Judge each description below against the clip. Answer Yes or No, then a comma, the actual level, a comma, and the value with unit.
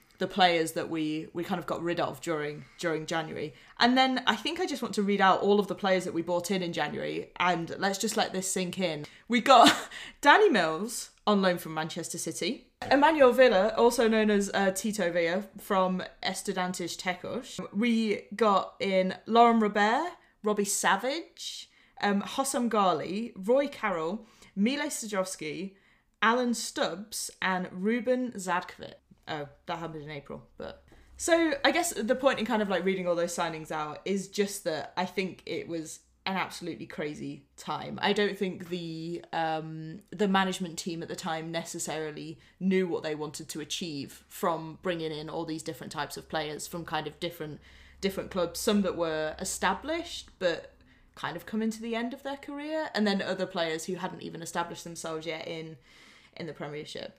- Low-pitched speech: No, medium, 185 Hz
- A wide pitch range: No, average, 4.7 semitones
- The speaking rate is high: No, average, 180 wpm